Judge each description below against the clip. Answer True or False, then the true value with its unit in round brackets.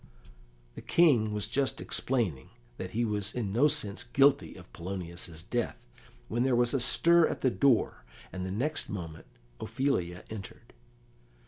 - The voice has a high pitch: False (110 Hz)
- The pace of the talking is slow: False (150 wpm)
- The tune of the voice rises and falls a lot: True (6.1 semitones)